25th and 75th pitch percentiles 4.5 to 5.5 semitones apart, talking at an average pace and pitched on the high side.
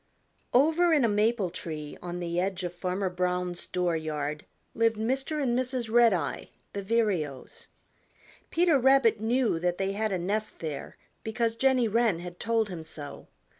Yes: average, 5.1 semitones; average, 160 wpm; high, 205 Hz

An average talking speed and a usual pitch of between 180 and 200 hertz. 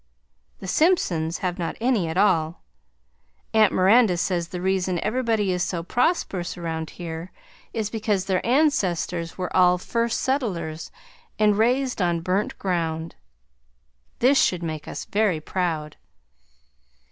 No: slow, 130 wpm; medium, 185 Hz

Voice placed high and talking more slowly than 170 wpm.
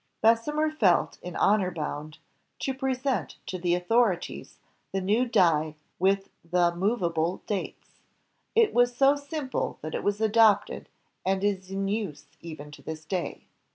Yes: high, 195 Hz; average, 150 wpm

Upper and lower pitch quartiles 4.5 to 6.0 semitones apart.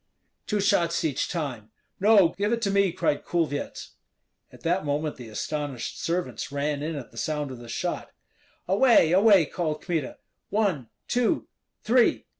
Yes: wide, 5.6 semitones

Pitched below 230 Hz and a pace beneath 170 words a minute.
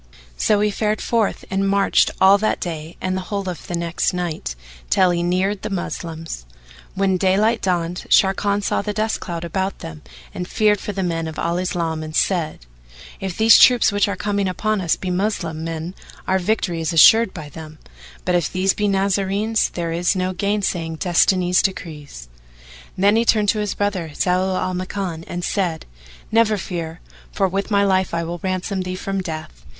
No: medium, 185 Hz; average, 185 wpm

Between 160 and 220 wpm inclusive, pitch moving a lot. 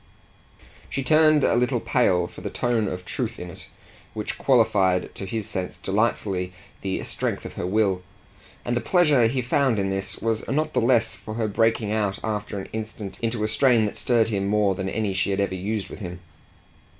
No: average, 200 wpm; average, 3.5 semitones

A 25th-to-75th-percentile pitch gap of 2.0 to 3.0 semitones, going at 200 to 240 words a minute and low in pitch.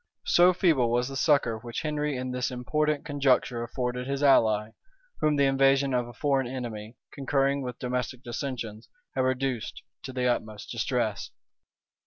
No: narrow, 2.4 semitones; average, 155 wpm; low, 130 Hz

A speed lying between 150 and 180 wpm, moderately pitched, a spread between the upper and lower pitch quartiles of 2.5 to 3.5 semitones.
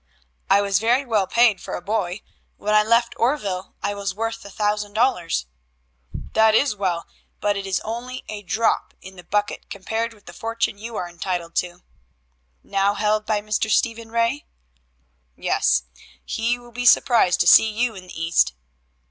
No: average, 175 wpm; high, 210 Hz; average, 3.0 semitones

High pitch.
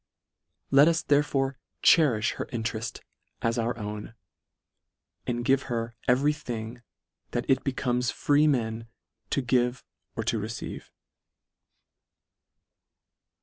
No: low, 120 Hz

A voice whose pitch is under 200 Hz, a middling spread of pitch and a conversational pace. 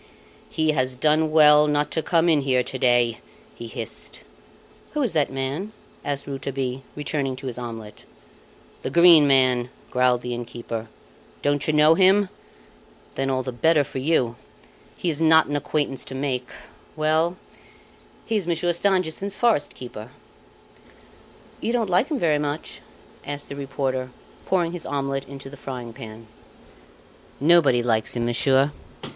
Yes: medium, 140 Hz; average, 3.9 semitones; average, 155 wpm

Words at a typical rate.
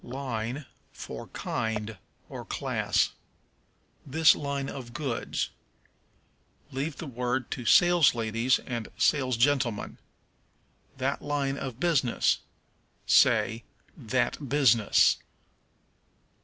No: slow, 85 wpm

